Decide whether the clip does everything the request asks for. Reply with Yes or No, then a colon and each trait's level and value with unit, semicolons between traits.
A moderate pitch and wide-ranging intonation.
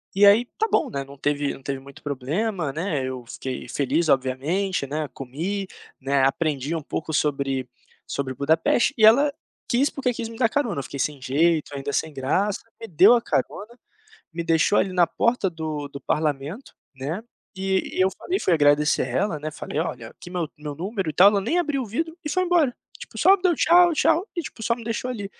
Yes: medium, 165 Hz; wide, 8.1 semitones